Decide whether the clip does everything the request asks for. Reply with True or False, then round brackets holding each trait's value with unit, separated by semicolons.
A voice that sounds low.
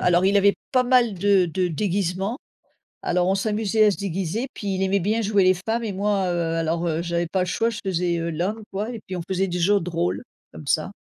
False (190 Hz)